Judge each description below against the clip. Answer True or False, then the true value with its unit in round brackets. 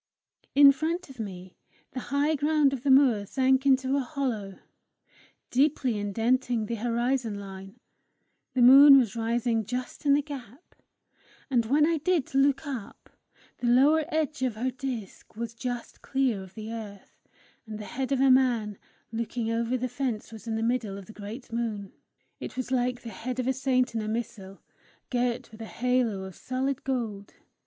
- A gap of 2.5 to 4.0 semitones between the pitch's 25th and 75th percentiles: True (3.3 semitones)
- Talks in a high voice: True (245 Hz)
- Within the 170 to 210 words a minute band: True (175 wpm)